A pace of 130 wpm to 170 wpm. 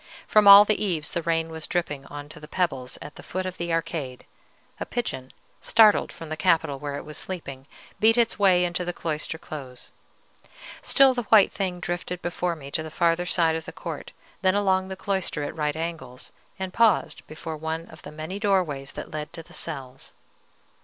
No: average, 200 wpm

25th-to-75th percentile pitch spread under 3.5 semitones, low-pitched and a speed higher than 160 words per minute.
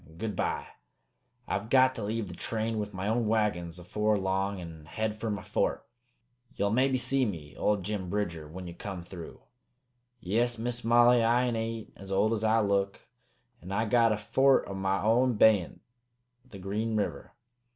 Yes: average, 2.9 semitones; low, 105 Hz; average, 175 wpm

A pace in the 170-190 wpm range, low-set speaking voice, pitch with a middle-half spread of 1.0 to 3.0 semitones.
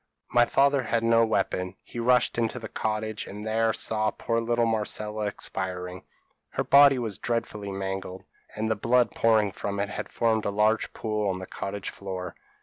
Yes: average, 175 wpm; low, 110 Hz; narrow, 2.5 semitones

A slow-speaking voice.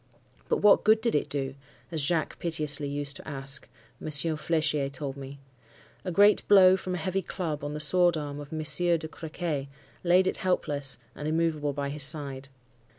No: average, 180 wpm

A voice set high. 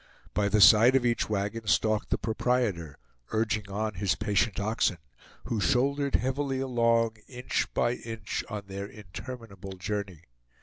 No: low, 110 Hz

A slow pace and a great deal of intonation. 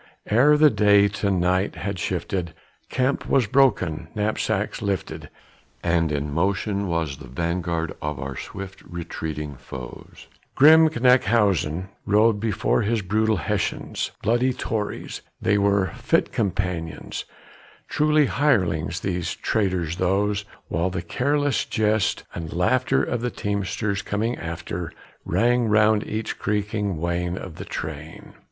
No: slow, 130 wpm; average, 4.5 semitones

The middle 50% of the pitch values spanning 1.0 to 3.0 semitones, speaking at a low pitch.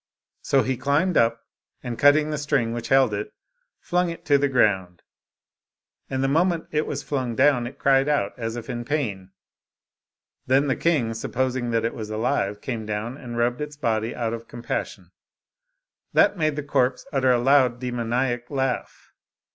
No: average, 3.6 semitones; low, 125 Hz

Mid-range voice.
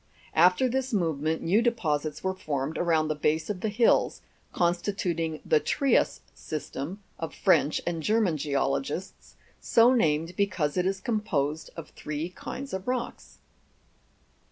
Yes: medium, 175 Hz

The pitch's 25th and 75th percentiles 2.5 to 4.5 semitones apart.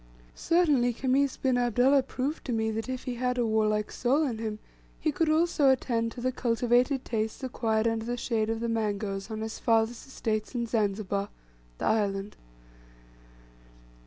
Yes: average, 2.8 semitones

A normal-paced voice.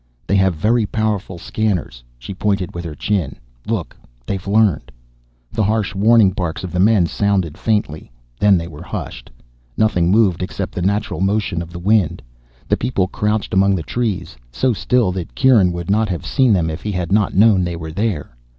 Yes: average, 185 wpm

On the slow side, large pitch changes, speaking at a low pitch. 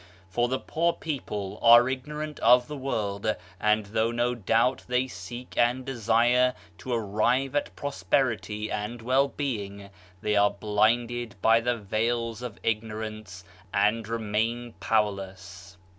No: slow, 130 wpm; average, 2.8 semitones; low, 115 Hz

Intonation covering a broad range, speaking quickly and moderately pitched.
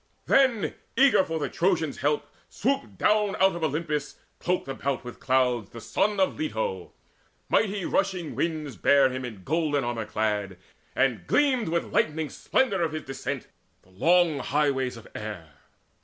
No: wide, 6.9 semitones; average, 155 wpm; medium, 150 Hz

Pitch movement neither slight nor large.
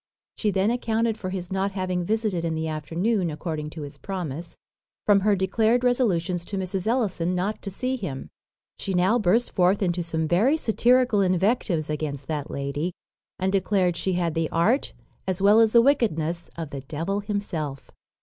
Yes: average, 4.3 semitones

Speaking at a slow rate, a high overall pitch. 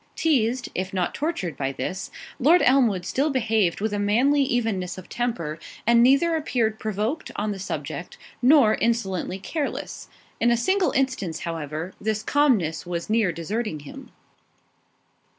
No: average, 145 wpm; high, 220 Hz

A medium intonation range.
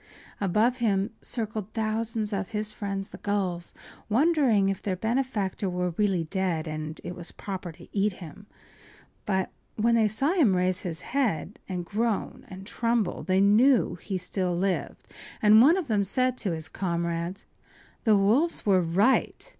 Yes: average, 3.5 semitones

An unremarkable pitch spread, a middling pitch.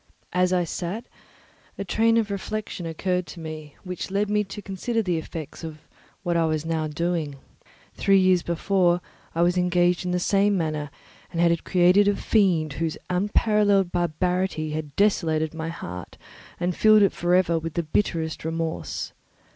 Yes: average, 3.2 semitones; medium, 175 Hz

